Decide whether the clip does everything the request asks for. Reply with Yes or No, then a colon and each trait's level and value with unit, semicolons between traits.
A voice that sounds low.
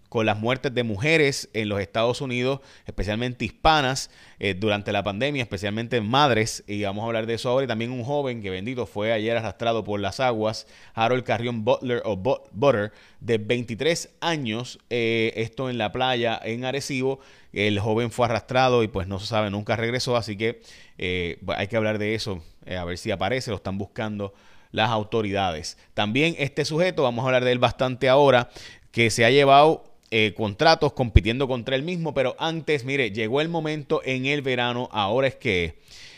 Yes: low, 115 Hz